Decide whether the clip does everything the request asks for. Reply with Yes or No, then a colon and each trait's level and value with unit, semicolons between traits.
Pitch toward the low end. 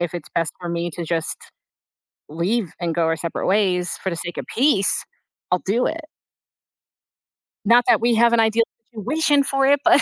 No: high, 195 Hz